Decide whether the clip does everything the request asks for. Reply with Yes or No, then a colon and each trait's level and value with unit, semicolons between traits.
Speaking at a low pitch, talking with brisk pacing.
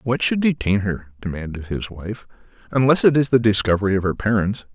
No: low, 110 Hz; average, 190 wpm